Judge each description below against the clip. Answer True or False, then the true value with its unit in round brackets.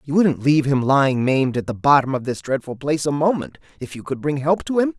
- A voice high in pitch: False (140 Hz)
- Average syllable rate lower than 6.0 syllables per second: False (6.2 syllables/s)